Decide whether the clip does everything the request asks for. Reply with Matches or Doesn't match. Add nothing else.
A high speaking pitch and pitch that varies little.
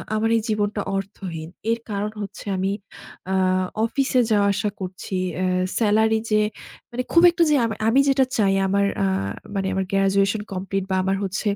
Matches